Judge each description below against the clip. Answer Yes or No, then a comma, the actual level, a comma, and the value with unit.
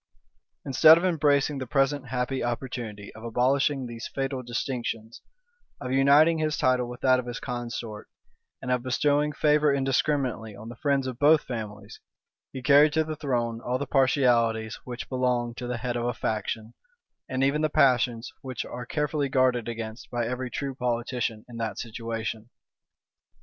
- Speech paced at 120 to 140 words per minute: No, average, 165 wpm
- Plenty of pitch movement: No, average, 2.9 semitones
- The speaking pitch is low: Yes, low, 125 Hz